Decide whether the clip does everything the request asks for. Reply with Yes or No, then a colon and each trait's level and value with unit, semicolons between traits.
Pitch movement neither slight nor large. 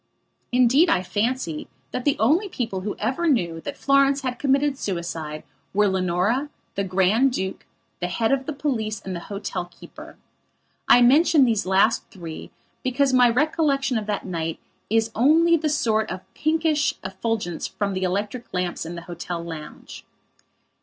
No: wide, 6.9 semitones